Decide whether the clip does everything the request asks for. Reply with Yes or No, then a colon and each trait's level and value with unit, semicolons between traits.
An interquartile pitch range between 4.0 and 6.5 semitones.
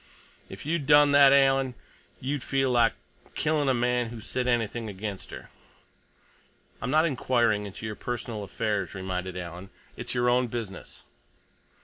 Yes: average, 4.4 semitones